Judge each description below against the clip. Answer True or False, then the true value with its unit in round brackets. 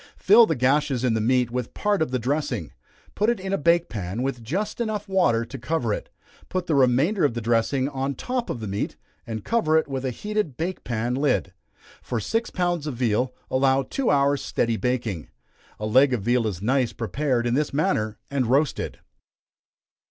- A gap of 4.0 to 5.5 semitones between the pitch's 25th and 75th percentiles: True (5.0 semitones)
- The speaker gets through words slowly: False (195 wpm)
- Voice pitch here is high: False (130 Hz)